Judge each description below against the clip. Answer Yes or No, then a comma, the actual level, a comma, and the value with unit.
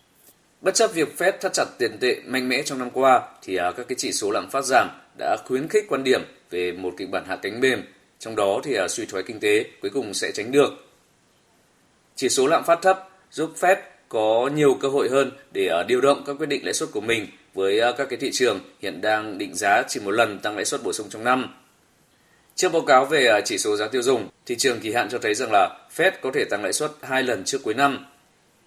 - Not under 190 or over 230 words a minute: No, average, 240 wpm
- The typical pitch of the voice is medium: Yes, medium, 150 Hz